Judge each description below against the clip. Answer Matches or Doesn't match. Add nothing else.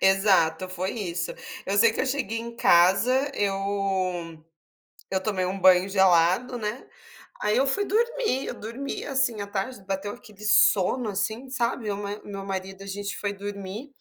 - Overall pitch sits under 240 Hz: Matches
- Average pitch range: Matches